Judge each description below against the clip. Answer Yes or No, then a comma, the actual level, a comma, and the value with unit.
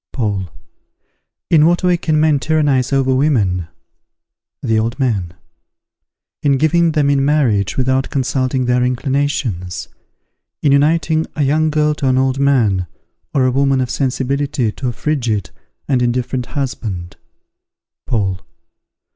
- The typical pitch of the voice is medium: No, low, 130 Hz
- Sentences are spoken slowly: Yes, slow, 130 wpm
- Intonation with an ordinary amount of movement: Yes, average, 3.5 semitones